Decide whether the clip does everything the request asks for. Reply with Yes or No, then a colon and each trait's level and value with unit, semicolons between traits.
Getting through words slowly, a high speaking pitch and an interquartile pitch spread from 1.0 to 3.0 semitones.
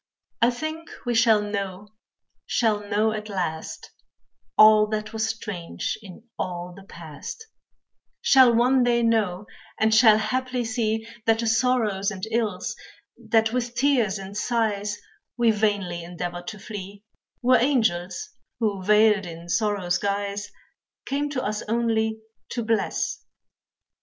Yes: slow, 130 wpm; high, 215 Hz; average, 2.7 semitones